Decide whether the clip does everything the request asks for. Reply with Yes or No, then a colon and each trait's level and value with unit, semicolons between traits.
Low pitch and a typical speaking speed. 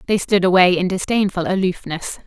No: medium, 185 Hz; average, 160 wpm